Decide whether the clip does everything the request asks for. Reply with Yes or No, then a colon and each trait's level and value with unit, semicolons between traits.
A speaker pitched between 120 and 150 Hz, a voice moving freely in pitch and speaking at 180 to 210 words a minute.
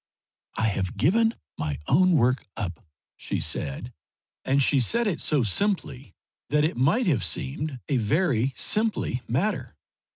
No: low, 135 Hz; wide, 7.9 semitones; average, 140 wpm